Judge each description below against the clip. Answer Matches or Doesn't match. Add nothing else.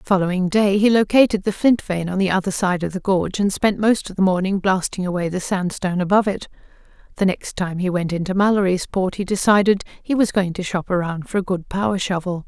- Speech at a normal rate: Doesn't match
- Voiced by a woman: Matches